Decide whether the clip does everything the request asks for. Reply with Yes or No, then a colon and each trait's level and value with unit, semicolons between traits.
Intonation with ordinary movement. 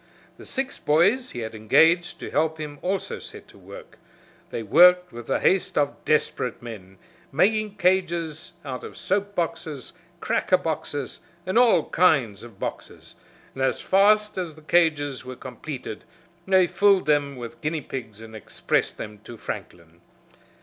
No: wide, 6.8 semitones